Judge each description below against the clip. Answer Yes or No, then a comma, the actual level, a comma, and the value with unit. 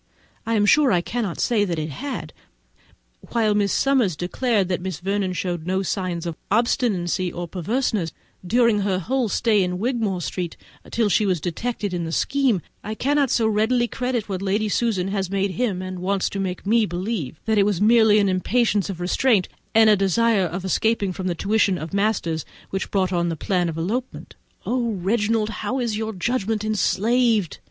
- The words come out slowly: No, average, 190 wpm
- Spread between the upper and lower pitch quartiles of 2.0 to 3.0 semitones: No, average, 3.9 semitones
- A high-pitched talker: Yes, high, 200 Hz